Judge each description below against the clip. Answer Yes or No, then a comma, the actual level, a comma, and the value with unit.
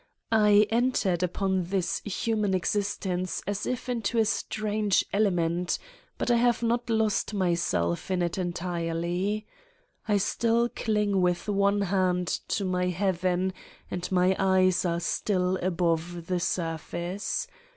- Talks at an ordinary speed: No, slow, 130 wpm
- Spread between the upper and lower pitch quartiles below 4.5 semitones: Yes, average, 2.9 semitones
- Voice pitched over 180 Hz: Yes, high, 190 Hz